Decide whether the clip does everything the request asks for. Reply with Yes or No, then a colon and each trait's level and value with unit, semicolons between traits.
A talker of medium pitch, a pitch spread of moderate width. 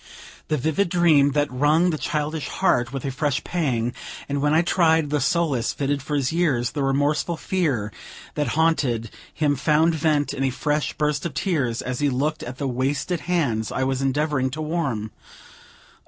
Yes: medium, 145 Hz; average, 3.3 semitones